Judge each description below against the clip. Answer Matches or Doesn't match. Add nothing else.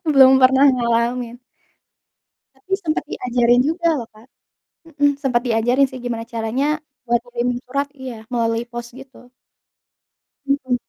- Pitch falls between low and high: Doesn't match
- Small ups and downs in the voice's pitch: Matches